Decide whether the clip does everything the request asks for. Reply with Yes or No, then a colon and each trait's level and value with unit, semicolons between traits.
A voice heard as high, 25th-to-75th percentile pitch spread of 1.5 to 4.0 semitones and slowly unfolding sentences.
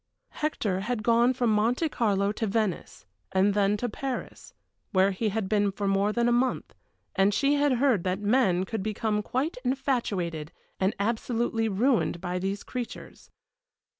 No: high, 215 Hz; average, 3.7 semitones; average, 160 wpm